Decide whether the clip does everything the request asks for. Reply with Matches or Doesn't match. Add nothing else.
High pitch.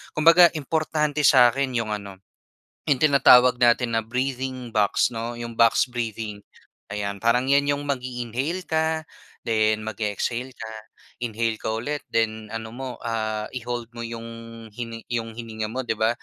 Doesn't match